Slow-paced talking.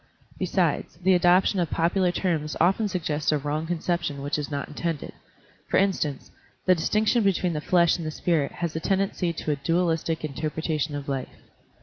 No: average, 175 wpm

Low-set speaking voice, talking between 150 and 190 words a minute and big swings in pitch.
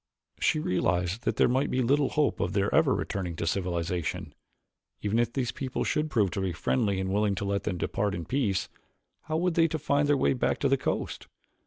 No: low, 105 Hz; fast, 205 wpm; wide, 7.3 semitones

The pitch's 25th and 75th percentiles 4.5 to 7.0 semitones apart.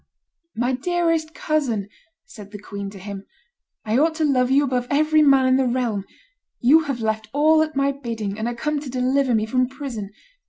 Yes: average, 4.8 semitones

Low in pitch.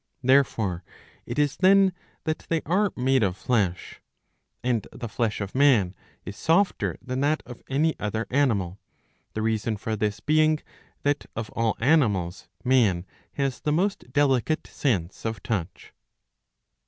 Yes: low, 125 Hz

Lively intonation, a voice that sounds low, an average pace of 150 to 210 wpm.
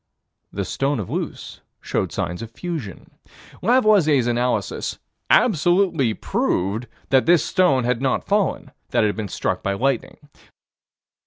No: wide, 7.6 semitones; low, 130 Hz; slow, 135 wpm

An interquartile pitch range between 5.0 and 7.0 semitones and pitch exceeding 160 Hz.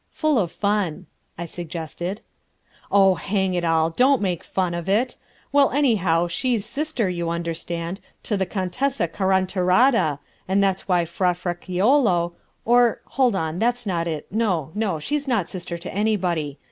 No: average, 4.4 semitones; medium, 185 Hz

